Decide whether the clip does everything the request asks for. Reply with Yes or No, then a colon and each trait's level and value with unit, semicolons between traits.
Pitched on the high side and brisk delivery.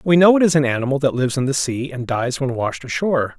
No: low, 135 Hz; fast, 285 wpm